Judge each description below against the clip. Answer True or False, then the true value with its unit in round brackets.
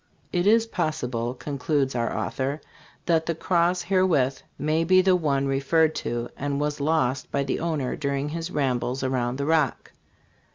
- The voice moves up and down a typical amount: True (3.8 semitones)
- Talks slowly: False (165 wpm)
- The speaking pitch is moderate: True (145 Hz)